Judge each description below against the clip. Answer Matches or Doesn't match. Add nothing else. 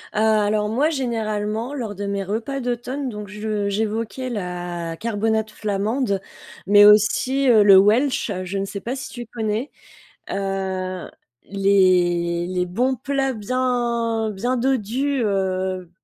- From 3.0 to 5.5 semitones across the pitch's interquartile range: Matches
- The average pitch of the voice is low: Doesn't match